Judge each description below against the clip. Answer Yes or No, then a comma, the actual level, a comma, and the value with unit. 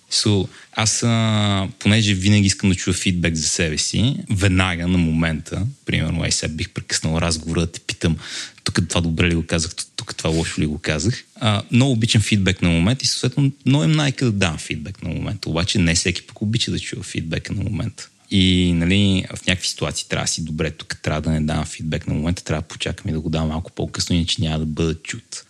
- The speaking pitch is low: Yes, very low, 90 Hz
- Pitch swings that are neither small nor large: Yes, average, 4.7 semitones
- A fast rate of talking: Yes, fast, 225 wpm